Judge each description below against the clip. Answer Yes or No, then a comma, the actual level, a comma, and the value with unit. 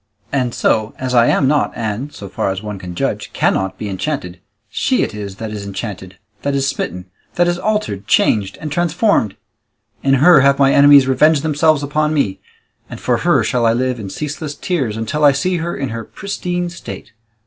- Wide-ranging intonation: Yes, wide, 6.3 semitones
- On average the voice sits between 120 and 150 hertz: Yes, low, 135 Hz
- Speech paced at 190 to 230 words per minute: Yes, average, 195 wpm